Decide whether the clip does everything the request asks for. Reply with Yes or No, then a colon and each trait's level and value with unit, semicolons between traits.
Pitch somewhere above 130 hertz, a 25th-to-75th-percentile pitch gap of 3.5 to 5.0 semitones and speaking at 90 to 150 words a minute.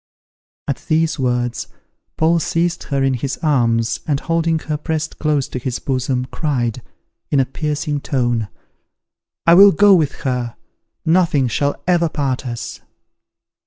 Yes: medium, 140 Hz; average, 4.2 semitones; average, 140 wpm